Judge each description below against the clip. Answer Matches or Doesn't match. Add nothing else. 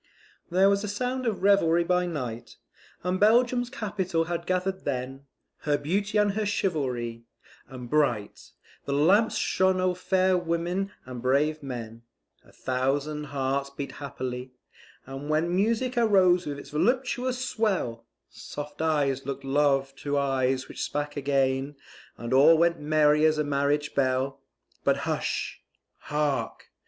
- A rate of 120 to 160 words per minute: Matches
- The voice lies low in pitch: Doesn't match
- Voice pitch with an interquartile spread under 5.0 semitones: Doesn't match